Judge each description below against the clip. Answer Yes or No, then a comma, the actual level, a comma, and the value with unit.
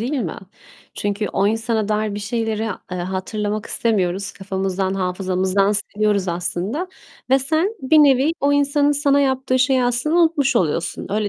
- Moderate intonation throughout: No, wide, 5.8 semitones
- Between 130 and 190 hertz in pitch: No, high, 215 Hz